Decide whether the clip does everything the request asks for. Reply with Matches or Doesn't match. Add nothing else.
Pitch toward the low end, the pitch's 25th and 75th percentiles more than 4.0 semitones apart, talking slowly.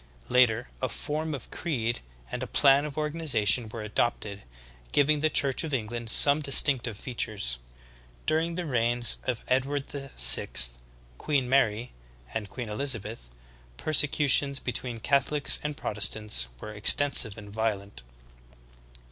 Matches